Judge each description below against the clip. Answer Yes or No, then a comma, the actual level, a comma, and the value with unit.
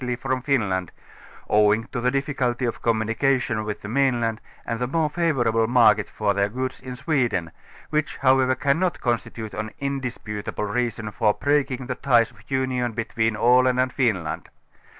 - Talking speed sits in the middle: Yes, average, 165 wpm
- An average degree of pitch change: Yes, average, 3.1 semitones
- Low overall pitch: Yes, low, 125 Hz